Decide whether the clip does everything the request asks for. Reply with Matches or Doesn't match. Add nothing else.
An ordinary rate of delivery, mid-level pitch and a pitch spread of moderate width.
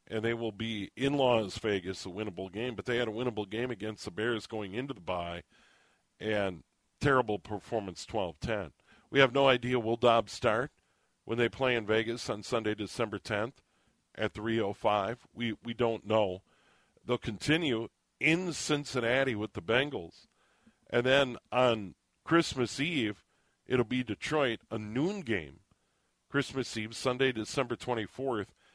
Doesn't match